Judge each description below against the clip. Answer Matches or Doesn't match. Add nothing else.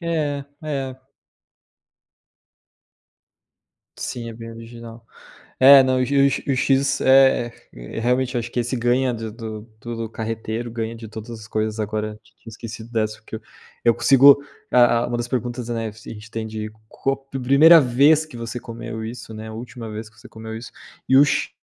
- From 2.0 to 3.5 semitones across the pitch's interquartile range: Matches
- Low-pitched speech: Matches